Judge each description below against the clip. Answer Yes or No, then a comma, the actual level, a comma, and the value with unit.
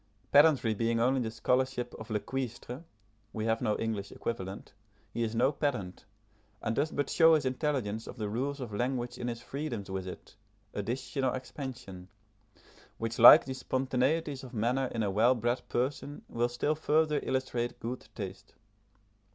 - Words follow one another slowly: No, average, 165 wpm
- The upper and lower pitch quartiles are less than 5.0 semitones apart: Yes, average, 3.1 semitones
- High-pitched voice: No, low, 120 Hz